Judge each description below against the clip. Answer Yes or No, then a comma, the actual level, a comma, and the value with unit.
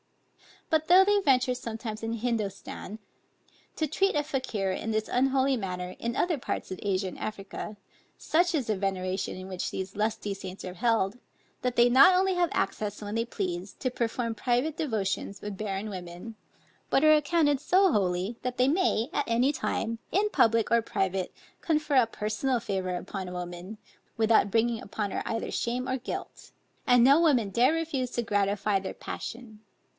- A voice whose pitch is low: No, high, 230 Hz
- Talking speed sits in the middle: Yes, average, 175 wpm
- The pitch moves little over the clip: No, average, 5.3 semitones